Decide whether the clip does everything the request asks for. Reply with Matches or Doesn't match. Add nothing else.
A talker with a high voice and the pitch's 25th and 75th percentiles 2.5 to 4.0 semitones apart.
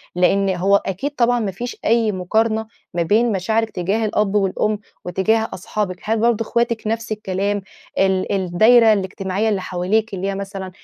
Matches